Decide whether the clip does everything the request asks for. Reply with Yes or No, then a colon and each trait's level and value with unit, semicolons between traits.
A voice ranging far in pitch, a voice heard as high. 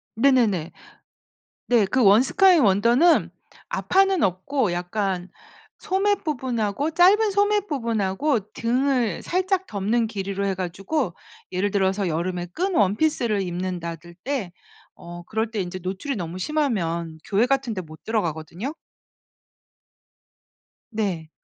Yes: wide, 7.1 semitones; high, 215 Hz